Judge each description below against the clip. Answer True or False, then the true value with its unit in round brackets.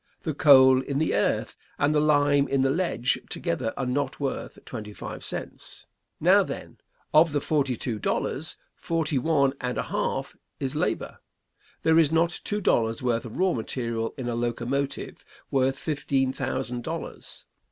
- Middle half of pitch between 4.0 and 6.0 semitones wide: False (3.3 semitones)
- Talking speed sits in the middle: True (165 wpm)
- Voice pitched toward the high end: False (135 Hz)